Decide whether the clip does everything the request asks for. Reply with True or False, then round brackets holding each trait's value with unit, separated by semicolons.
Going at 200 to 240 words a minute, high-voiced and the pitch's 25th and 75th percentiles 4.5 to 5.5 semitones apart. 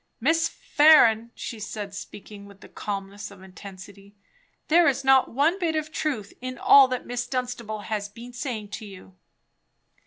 False (160 wpm; 230 Hz; 4.9 semitones)